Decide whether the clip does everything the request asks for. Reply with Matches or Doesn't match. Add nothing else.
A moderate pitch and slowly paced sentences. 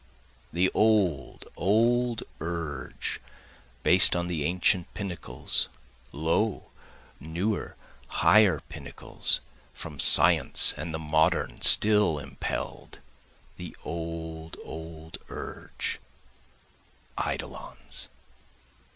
Doesn't match